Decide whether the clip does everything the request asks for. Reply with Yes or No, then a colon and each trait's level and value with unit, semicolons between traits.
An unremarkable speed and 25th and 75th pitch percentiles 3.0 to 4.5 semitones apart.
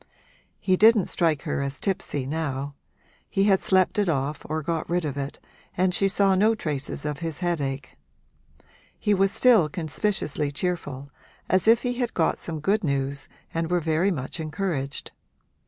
No: average, 165 wpm; average, 5.2 semitones